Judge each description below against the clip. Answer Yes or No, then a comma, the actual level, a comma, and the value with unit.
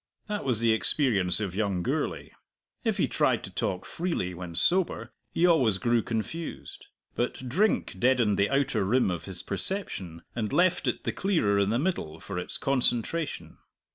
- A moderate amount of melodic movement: No, wide, 8.5 semitones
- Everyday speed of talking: Yes, average, 170 wpm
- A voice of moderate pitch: No, low, 115 Hz